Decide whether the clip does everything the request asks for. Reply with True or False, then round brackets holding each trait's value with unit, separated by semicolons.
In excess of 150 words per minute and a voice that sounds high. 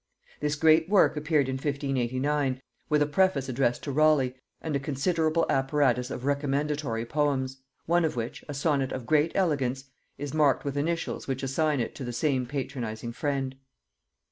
False (165 wpm; 140 Hz)